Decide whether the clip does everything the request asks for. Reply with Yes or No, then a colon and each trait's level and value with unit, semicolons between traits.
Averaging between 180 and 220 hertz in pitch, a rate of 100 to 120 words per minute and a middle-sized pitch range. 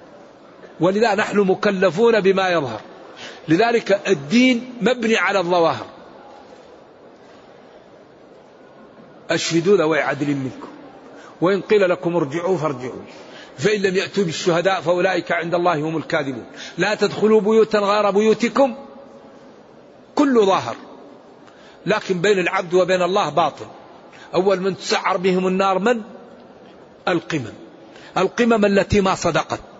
Yes: high, 190 Hz; average, 105 wpm; average, 3.6 semitones